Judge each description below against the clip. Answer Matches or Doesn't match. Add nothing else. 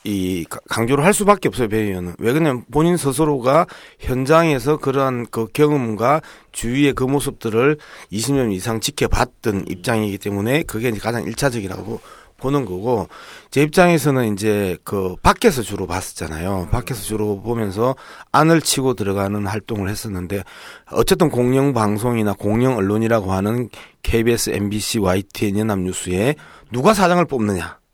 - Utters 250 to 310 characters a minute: Doesn't match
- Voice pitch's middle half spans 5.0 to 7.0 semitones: Matches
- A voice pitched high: Doesn't match